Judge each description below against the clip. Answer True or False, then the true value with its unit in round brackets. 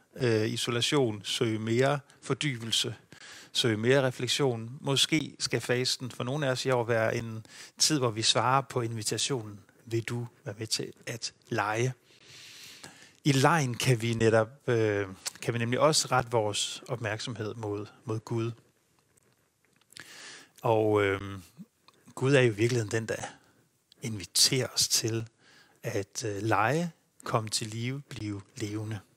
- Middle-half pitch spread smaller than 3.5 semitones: True (3.1 semitones)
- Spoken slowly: True (135 wpm)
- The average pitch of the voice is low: True (120 Hz)